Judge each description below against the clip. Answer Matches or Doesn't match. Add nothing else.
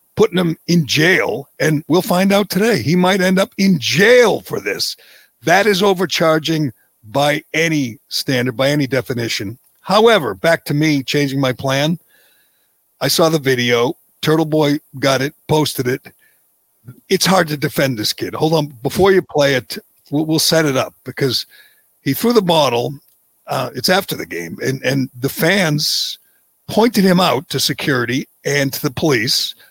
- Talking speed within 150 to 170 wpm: Matches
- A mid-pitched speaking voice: Matches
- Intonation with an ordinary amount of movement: Matches